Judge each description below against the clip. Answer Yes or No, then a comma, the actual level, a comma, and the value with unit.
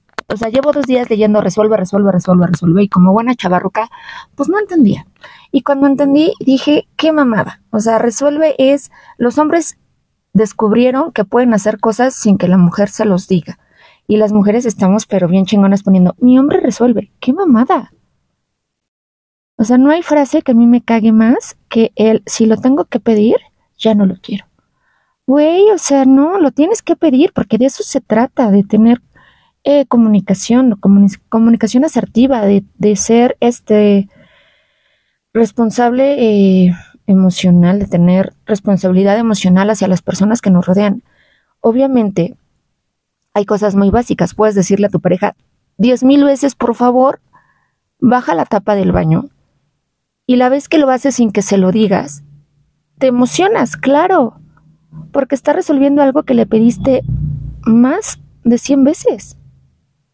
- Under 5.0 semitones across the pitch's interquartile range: No, average, 5.3 semitones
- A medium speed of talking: Yes, average, 160 wpm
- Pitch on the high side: Yes, high, 225 Hz